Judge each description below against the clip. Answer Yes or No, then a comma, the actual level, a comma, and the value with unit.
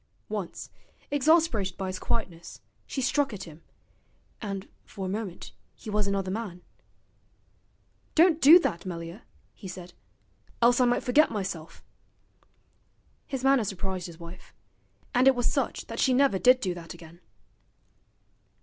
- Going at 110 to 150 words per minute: Yes, average, 140 wpm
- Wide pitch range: Yes, wide, 5.8 semitones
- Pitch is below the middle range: No, high, 200 Hz